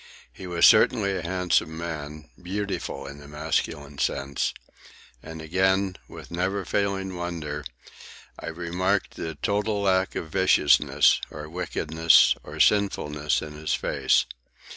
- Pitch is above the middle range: No, very low, 85 Hz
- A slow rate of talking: Yes, slow, 120 wpm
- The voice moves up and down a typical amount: Yes, average, 3.8 semitones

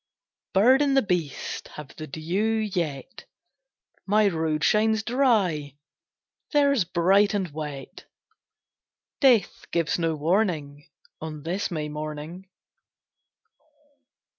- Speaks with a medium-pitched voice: Yes, medium, 175 Hz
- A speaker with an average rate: No, slow, 100 wpm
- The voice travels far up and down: Yes, wide, 5.9 semitones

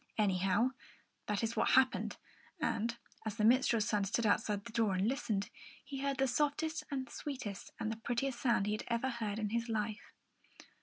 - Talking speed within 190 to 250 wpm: Yes, average, 195 wpm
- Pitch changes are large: No, average, 3.7 semitones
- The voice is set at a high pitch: Yes, high, 230 Hz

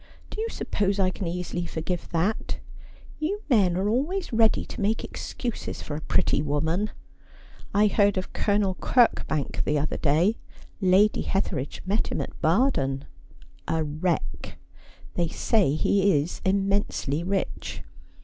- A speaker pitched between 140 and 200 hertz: Yes, high, 190 Hz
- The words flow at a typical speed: Yes, average, 145 wpm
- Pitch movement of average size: Yes, average, 4.7 semitones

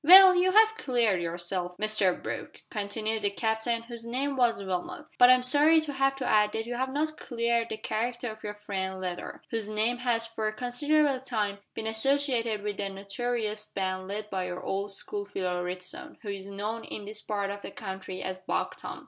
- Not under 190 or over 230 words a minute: Yes, average, 200 wpm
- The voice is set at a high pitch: Yes, high, 220 Hz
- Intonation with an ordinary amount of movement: Yes, average, 3.7 semitones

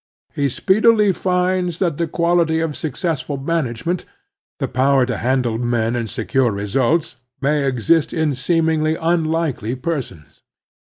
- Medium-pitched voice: Yes, medium, 150 Hz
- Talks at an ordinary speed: No, slow, 130 wpm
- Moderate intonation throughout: Yes, average, 5.0 semitones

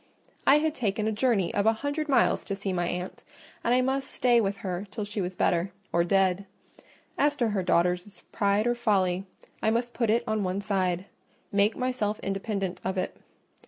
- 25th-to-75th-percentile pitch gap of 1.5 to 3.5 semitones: No, average, 3.9 semitones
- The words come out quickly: No, average, 190 wpm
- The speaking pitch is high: Yes, high, 205 Hz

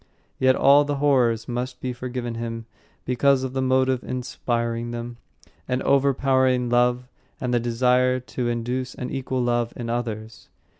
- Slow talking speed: No, average, 150 wpm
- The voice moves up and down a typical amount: No, narrow, 1.5 semitones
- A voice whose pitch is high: No, low, 125 Hz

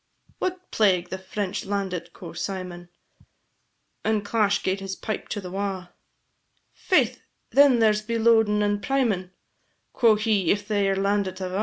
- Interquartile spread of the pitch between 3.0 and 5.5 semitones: No, narrow, 2.4 semitones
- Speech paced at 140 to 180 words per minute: Yes, average, 150 wpm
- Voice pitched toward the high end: Yes, high, 200 Hz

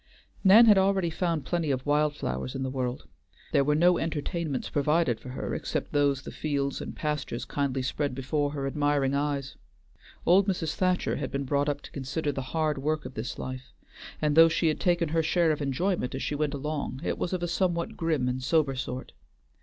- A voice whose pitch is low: No, medium, 145 Hz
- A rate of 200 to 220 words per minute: Yes, fast, 205 wpm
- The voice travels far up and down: No, average, 3.4 semitones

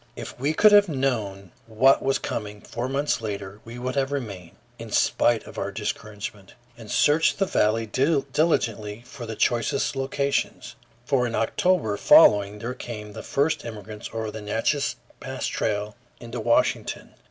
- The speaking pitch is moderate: No, low, 115 Hz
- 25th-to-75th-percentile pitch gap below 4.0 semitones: No, average, 4.5 semitones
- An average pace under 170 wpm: Yes, average, 155 wpm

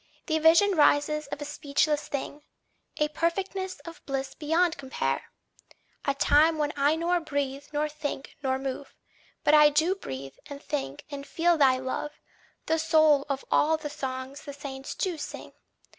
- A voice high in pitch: Yes, very high, 295 Hz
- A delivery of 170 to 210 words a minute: No, average, 160 wpm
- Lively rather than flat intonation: No, narrow, 2.5 semitones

